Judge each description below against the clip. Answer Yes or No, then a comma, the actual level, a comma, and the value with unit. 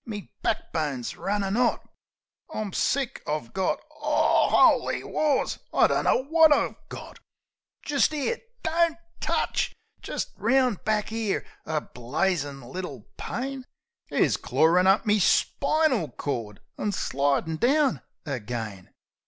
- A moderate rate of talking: No, slow, 120 wpm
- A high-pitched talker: Yes, high, 200 Hz